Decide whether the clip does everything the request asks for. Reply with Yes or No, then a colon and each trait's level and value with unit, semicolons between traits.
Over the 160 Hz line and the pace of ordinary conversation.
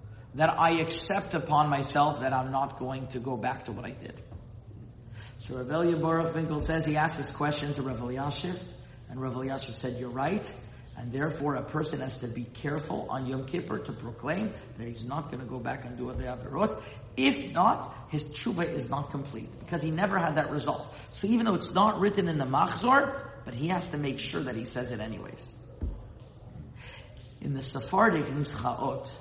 No: low, 135 Hz; average, 195 wpm